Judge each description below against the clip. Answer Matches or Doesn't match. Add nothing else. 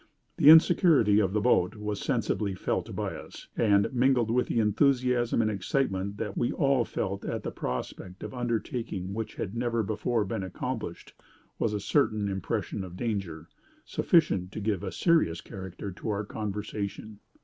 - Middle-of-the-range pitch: Doesn't match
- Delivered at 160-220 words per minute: Matches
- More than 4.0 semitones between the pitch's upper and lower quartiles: Doesn't match